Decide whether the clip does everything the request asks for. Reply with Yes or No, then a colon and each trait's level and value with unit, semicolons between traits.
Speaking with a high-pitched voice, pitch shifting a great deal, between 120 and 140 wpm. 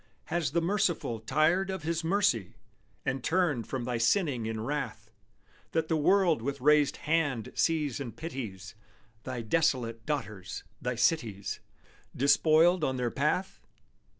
No: medium, 140 Hz; wide, 5.9 semitones; slow, 135 wpm